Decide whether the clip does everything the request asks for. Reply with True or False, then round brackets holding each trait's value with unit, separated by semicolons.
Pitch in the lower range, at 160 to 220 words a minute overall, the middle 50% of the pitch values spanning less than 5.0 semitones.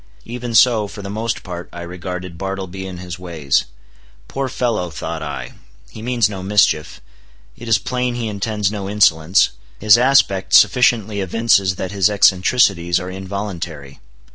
False (95 Hz; 150 wpm; 3.7 semitones)